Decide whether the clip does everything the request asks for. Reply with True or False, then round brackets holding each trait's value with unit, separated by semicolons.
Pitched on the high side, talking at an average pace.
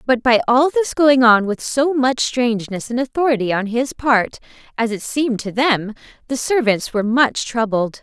True (245 Hz; 185 wpm)